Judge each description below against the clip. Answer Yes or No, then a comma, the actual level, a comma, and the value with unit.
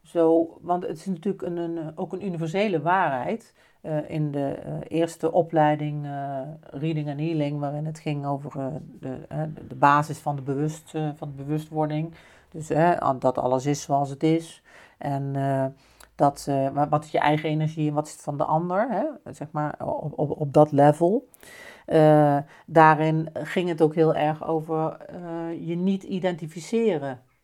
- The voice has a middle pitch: Yes, medium, 155 Hz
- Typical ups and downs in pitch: No, narrow, 2.2 semitones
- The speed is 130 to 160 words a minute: No, average, 175 wpm